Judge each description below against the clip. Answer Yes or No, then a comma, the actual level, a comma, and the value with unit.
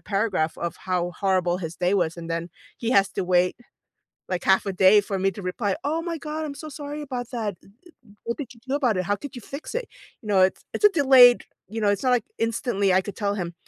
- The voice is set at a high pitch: Yes, high, 205 Hz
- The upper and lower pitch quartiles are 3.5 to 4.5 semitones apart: No, wide, 5.5 semitones